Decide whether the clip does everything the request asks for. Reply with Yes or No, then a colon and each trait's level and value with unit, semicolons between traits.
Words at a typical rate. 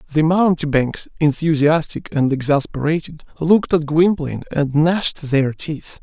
No: slow, 120 wpm